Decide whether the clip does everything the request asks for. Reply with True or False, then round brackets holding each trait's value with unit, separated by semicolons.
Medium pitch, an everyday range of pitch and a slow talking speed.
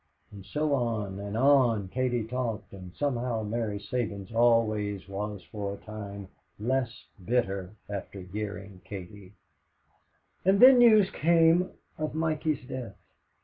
False (110 Hz; 4.5 semitones; 125 wpm)